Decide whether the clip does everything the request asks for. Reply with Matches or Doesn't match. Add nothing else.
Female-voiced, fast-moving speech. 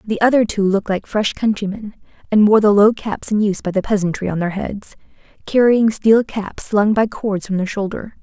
Matches